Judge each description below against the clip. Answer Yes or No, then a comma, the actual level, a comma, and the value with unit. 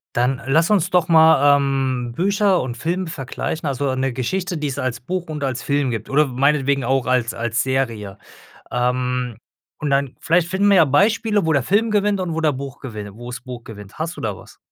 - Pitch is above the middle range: No, medium, 140 Hz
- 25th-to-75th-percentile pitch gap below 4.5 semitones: No, average, 4.9 semitones